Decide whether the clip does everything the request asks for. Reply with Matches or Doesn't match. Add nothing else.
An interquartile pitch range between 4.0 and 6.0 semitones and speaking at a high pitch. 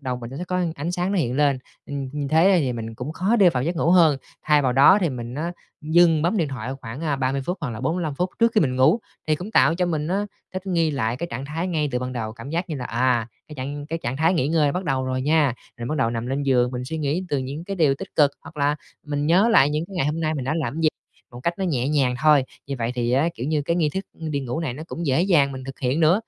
Doesn't match